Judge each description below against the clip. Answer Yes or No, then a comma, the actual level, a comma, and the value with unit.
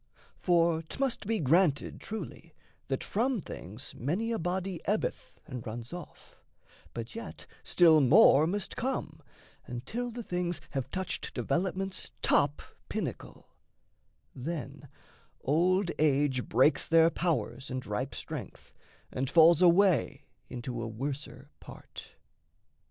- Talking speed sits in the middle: No, slow, 120 wpm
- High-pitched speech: No, medium, 165 Hz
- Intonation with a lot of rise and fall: Yes, wide, 5.8 semitones